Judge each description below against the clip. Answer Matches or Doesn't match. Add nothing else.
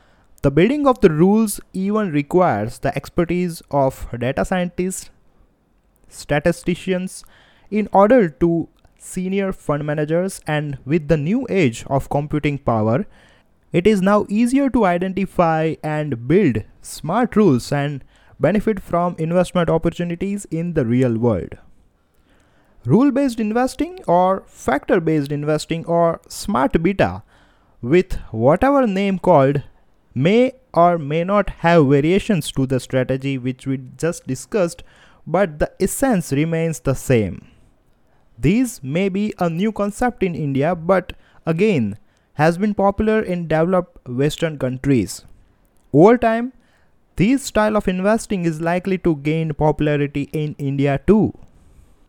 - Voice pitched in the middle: Matches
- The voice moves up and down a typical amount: Doesn't match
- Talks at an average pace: Doesn't match